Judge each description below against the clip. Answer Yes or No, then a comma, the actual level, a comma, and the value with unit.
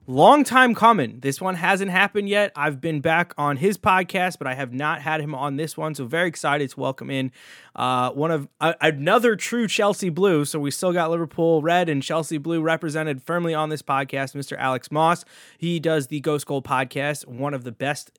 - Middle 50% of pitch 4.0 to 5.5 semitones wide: No, average, 3.6 semitones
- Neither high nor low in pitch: Yes, medium, 155 Hz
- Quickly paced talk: Yes, fast, 210 wpm